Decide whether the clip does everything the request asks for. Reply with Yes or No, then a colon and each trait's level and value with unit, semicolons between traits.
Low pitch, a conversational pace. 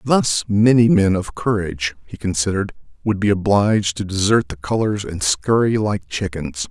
Yes: low, 100 Hz; average, 160 wpm